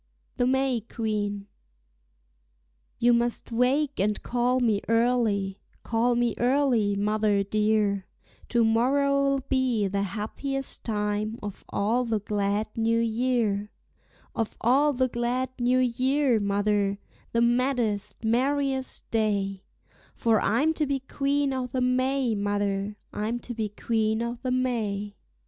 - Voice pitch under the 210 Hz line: No, high, 230 Hz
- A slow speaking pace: Yes, slow, 125 wpm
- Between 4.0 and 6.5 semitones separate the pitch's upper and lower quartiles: No, average, 3.6 semitones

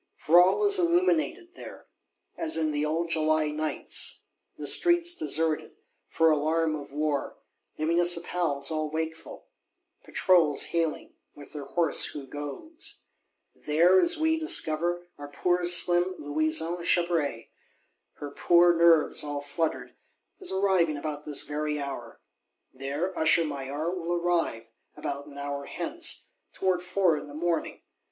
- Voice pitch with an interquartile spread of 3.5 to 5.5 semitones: No, average, 3.1 semitones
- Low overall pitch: No, medium, 160 Hz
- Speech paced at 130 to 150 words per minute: Yes, slow, 135 wpm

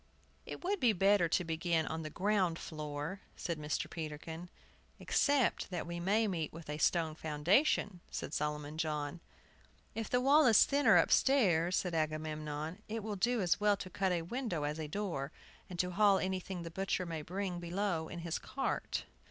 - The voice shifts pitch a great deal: No, average, 4.2 semitones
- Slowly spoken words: No, average, 175 wpm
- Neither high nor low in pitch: Yes, medium, 175 Hz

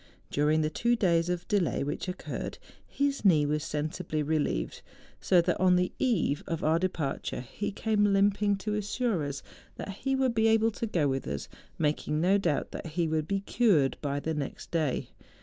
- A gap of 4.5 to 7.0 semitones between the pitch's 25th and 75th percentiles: Yes, average, 5.2 semitones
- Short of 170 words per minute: No, average, 185 wpm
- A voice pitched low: No, medium, 175 Hz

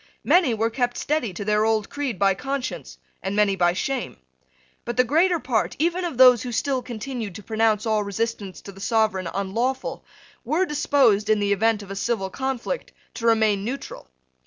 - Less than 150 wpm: No, average, 185 wpm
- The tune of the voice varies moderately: Yes, average, 4.4 semitones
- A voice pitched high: Yes, high, 225 Hz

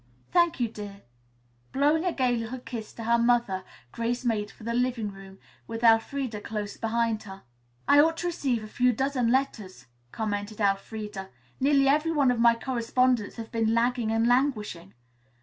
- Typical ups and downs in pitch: Yes, average, 3.1 semitones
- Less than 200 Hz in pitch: No, high, 235 Hz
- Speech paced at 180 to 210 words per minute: No, average, 165 wpm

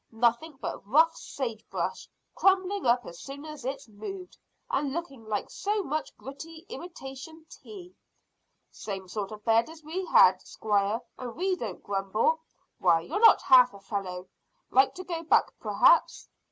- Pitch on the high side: Yes, very high, 270 Hz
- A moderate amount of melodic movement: No, wide, 7.6 semitones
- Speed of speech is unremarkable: Yes, average, 155 wpm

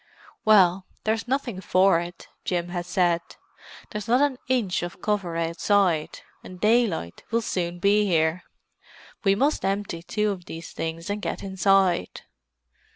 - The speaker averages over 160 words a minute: No, average, 145 wpm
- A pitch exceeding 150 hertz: Yes, high, 190 Hz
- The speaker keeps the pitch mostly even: No, average, 3.4 semitones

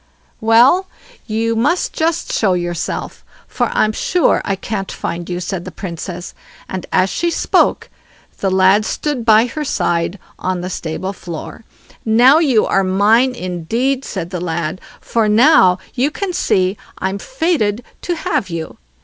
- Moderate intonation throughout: No, wide, 5.9 semitones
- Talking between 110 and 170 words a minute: Yes, average, 150 wpm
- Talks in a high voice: Yes, high, 210 Hz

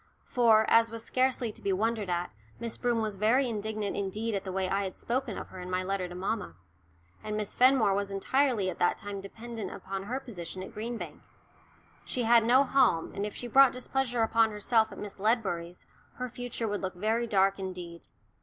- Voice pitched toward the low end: No, high, 215 Hz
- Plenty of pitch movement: No, average, 3.5 semitones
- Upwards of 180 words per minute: Yes, fast, 205 wpm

